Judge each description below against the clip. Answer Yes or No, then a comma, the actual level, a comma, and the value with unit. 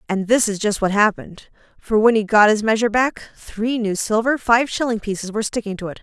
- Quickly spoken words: Yes, fast, 230 wpm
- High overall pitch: Yes, high, 215 Hz